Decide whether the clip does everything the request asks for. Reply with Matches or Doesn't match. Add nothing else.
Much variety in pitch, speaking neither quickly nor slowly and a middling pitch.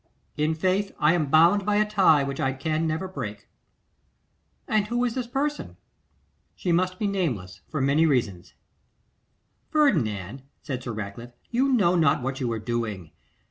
Matches